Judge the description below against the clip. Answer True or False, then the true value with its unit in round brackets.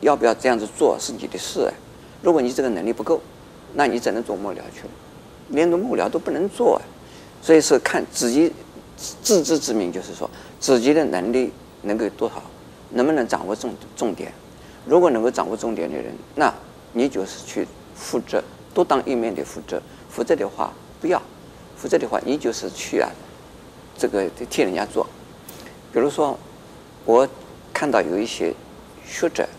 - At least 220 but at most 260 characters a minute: True (255 characters per minute)